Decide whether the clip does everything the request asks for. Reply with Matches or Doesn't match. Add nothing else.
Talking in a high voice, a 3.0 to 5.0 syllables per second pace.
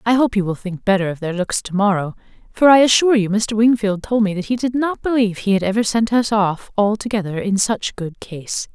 Doesn't match